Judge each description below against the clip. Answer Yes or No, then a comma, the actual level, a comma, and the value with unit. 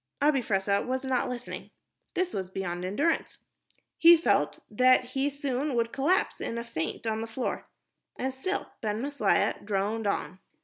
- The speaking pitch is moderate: No, high, 245 Hz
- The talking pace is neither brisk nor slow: Yes, average, 160 wpm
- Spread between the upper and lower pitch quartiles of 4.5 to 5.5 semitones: Yes, average, 4.9 semitones